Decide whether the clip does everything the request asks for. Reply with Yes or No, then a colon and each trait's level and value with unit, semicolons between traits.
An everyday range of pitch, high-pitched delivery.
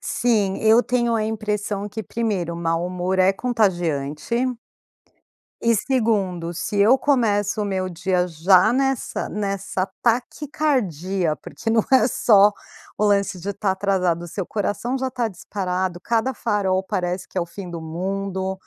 Yes: average, 3.7 semitones; high, 200 Hz